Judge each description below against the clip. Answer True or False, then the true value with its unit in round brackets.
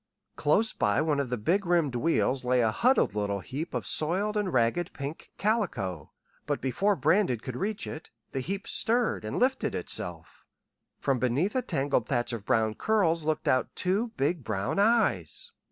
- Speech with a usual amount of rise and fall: False (8.5 semitones)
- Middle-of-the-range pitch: True (150 Hz)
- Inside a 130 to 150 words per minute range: False (170 wpm)